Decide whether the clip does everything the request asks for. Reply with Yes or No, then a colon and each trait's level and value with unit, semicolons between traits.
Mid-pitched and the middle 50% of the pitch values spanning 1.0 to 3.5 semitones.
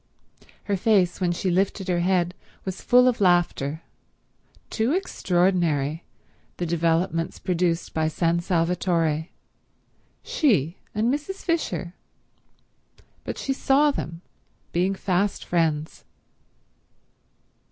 Yes: medium, 180 Hz; average, 3.2 semitones